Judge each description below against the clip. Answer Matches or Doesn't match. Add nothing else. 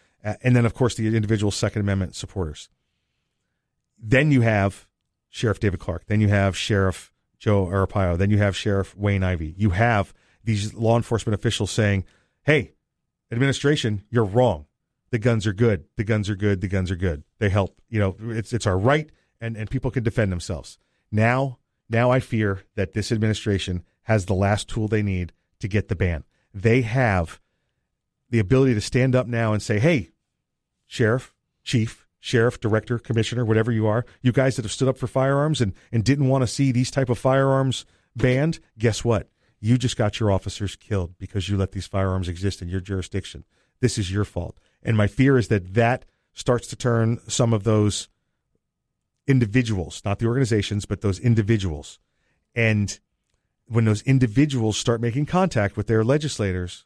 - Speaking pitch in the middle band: Doesn't match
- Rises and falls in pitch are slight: Doesn't match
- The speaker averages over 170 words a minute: Matches